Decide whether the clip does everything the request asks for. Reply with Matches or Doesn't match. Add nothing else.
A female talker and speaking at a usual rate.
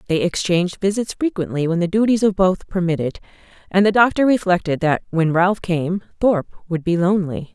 Matches